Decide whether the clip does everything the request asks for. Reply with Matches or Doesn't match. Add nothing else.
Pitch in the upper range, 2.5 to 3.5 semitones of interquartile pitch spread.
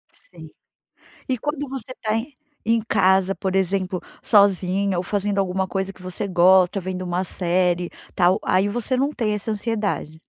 Matches